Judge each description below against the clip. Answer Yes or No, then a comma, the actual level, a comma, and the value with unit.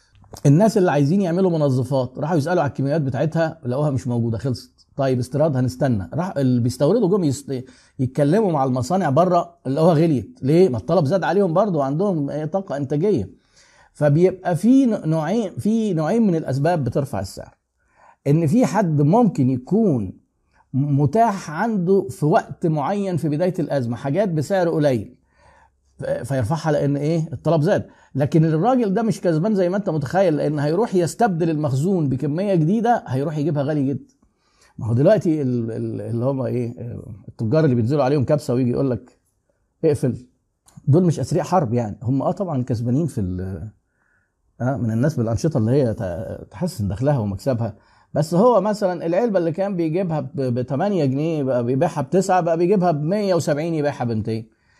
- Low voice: No, medium, 150 Hz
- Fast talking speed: Yes, fast, 150 wpm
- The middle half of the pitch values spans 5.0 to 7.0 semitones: Yes, wide, 5.6 semitones